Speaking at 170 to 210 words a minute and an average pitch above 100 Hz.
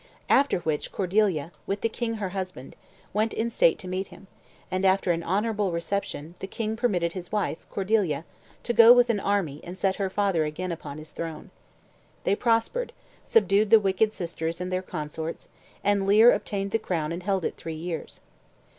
Yes: average, 180 wpm; high, 190 Hz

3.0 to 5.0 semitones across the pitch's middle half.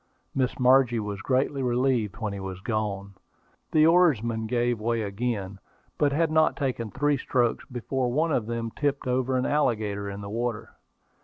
Yes: average, 3.9 semitones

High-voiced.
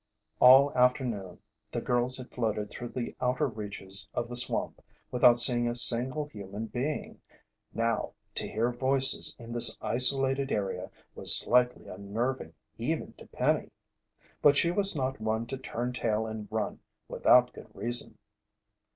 No: low, 120 Hz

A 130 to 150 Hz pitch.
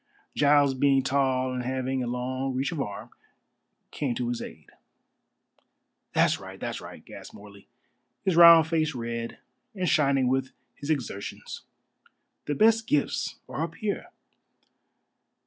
Yes: low, 135 Hz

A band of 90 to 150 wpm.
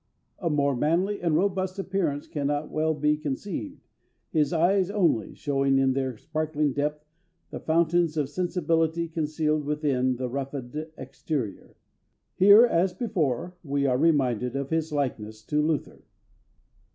Yes: slow, 135 wpm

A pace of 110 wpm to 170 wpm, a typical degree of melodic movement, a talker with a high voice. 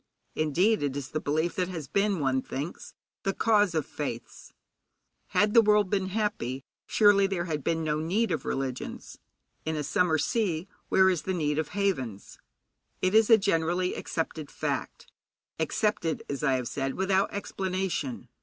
No: average, 165 wpm; average, 4.9 semitones; medium, 170 Hz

